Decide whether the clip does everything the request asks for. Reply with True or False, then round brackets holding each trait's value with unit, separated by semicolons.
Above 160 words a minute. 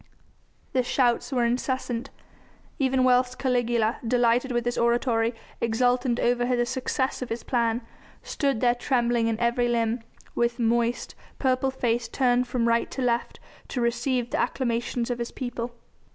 False (150 wpm)